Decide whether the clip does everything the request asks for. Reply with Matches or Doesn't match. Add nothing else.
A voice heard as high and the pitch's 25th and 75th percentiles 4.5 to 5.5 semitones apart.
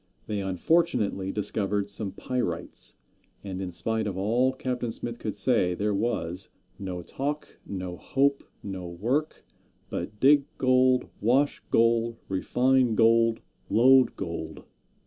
Doesn't match